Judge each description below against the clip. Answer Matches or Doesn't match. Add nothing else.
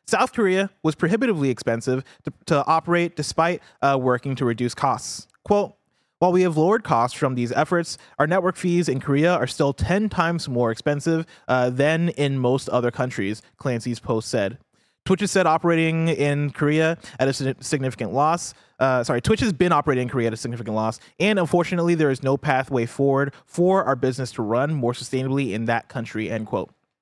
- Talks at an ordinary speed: Matches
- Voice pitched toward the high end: Doesn't match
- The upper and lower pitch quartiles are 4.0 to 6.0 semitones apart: Matches